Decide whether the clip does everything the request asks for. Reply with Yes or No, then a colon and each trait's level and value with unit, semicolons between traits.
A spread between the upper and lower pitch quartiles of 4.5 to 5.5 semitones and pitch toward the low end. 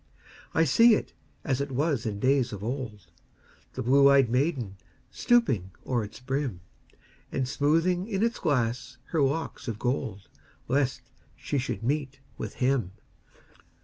No: average, 4.0 semitones; low, 130 Hz